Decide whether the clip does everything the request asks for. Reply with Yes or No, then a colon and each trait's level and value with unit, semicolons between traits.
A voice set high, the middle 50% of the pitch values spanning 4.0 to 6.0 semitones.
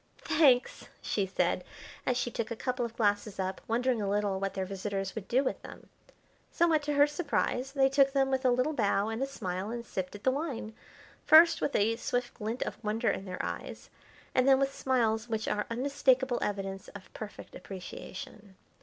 Yes: high, 230 Hz; average, 4.6 semitones